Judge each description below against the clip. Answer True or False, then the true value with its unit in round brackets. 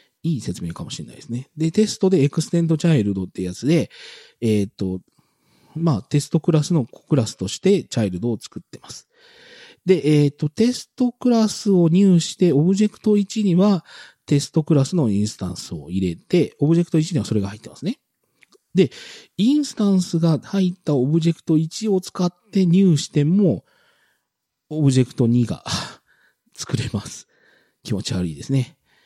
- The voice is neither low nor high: True (160 Hz)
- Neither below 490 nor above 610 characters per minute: False (340 characters per minute)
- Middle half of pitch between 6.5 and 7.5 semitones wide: True (6.9 semitones)